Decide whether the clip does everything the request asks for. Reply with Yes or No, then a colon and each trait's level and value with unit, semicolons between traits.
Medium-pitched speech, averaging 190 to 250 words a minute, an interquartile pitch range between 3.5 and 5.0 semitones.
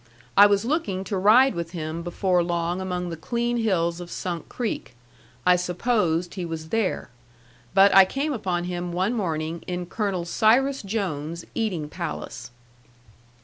No: medium, 180 Hz; average, 150 wpm; average, 3.9 semitones